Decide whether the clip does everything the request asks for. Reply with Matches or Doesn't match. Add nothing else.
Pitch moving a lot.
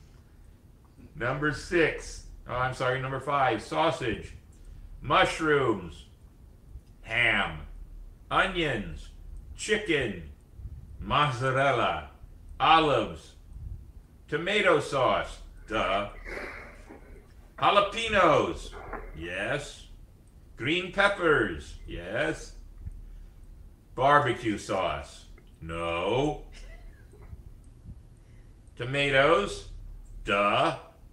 Matches